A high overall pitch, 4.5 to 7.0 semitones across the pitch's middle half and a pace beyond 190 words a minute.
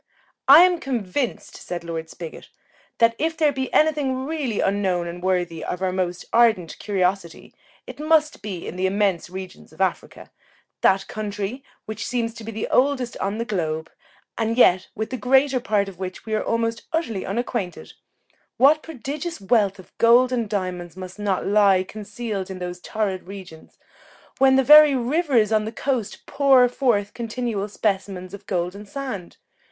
No: high, 215 Hz; average, 5.3 semitones; average, 170 wpm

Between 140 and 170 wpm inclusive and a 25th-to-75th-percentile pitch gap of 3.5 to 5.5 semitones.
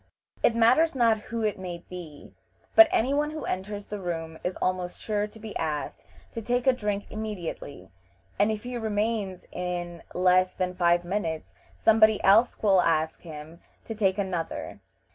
Yes: average, 165 wpm; average, 4.0 semitones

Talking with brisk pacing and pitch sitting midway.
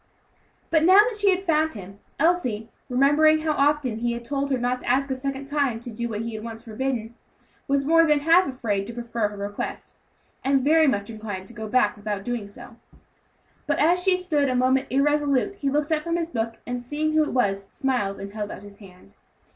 No: fast, 220 wpm; very high, 255 Hz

